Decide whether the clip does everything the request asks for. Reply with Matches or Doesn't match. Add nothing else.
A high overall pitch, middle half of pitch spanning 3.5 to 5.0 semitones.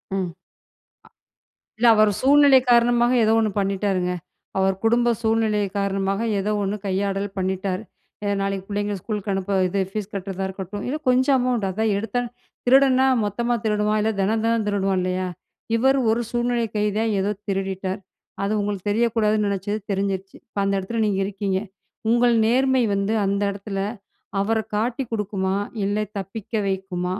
Doesn't match